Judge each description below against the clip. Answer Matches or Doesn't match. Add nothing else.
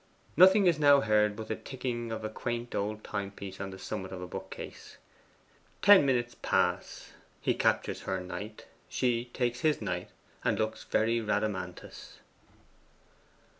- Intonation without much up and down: Doesn't match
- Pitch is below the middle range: Matches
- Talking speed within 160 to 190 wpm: Doesn't match